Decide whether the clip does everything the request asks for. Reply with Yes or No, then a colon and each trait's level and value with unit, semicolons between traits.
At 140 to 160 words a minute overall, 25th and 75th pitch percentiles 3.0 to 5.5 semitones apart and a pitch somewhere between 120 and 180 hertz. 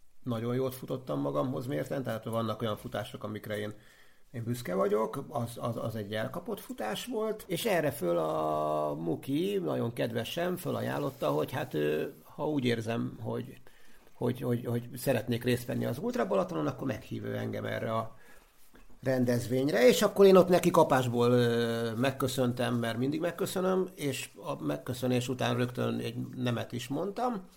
Yes: average, 150 wpm; average, 4.5 semitones; low, 125 Hz